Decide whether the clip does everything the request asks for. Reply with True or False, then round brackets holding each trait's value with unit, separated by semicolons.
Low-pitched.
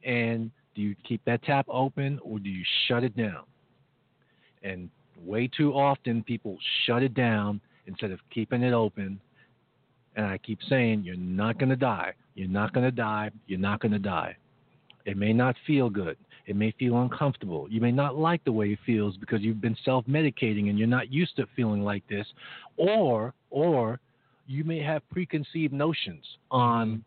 True (120 Hz)